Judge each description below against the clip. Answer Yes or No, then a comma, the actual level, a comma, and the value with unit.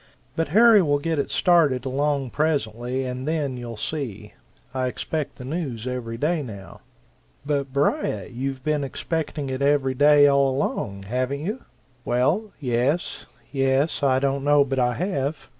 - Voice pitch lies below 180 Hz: Yes, medium, 140 Hz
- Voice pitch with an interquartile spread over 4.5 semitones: No, average, 2.8 semitones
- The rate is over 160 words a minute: No, average, 155 wpm